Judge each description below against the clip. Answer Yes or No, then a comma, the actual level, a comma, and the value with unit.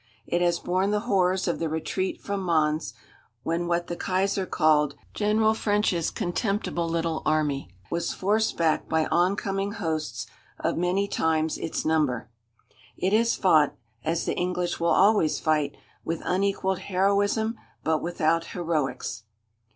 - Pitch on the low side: No, medium, 175 Hz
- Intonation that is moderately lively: Yes, average, 3.6 semitones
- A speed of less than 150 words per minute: Yes, average, 140 wpm